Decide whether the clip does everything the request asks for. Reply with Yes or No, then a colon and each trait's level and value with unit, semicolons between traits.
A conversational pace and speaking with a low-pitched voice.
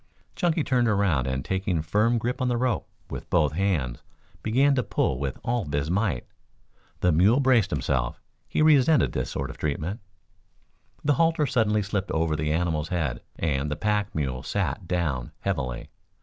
Yes: average, 165 wpm; very low, 95 Hz